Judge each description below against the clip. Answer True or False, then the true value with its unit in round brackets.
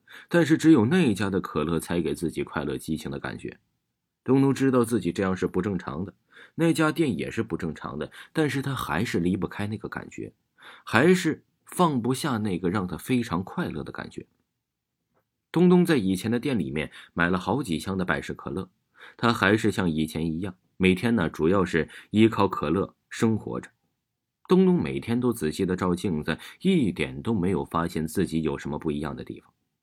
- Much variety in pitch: True (7.4 semitones)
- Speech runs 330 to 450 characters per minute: False (280 characters per minute)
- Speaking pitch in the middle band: False (95 Hz)